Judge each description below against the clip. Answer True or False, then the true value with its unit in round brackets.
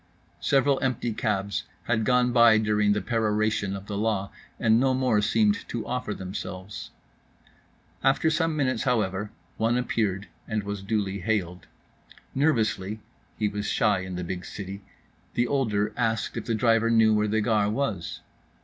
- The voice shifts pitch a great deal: False (3.1 semitones)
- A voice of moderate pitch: False (110 Hz)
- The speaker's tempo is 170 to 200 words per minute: False (155 wpm)